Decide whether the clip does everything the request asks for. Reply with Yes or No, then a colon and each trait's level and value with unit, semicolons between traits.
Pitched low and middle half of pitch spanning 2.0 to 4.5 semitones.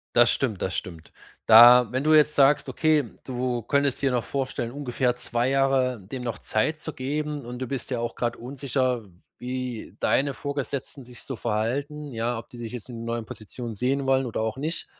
Yes: low, 125 Hz; average, 2.7 semitones